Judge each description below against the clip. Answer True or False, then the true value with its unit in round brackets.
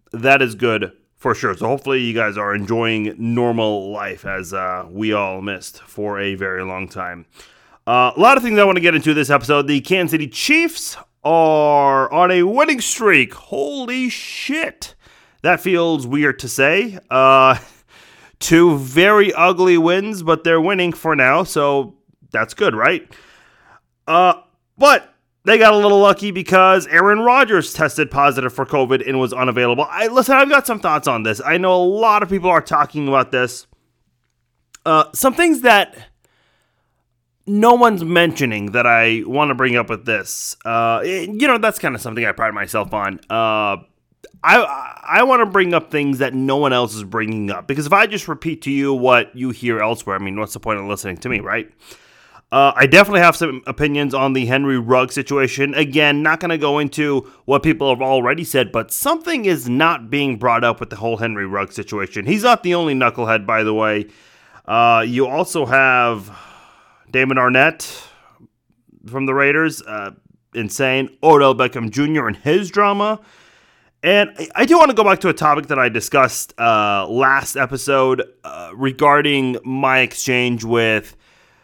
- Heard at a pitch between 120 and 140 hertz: True (135 Hz)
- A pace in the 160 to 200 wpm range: True (180 wpm)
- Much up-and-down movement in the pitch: True (6.6 semitones)